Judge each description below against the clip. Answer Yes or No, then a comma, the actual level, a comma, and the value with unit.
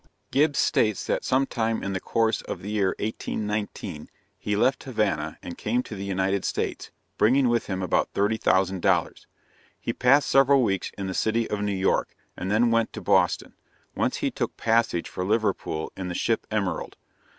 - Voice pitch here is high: No, low, 105 Hz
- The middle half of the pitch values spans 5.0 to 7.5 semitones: No, average, 3.2 semitones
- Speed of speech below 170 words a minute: No, average, 175 wpm